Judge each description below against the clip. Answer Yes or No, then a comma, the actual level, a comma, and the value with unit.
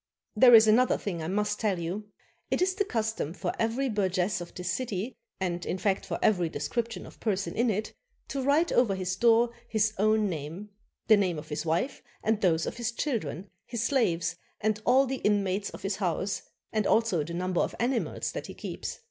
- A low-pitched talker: No, high, 210 Hz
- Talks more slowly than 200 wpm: No, fast, 205 wpm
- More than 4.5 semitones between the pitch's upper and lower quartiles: No, average, 4.2 semitones